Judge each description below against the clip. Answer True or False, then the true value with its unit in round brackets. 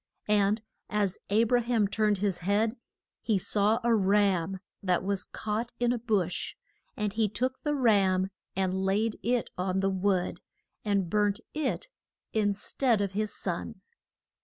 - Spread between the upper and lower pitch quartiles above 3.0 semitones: False (2.6 semitones)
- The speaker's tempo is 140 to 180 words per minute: True (155 wpm)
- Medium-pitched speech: False (205 Hz)